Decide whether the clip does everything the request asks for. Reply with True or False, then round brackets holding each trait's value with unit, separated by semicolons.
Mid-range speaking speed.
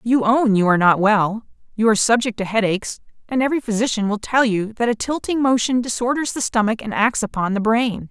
False (215 wpm)